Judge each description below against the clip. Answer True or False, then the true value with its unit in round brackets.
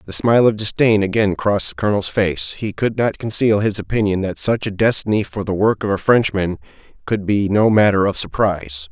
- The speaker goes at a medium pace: False (210 wpm)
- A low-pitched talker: True (100 Hz)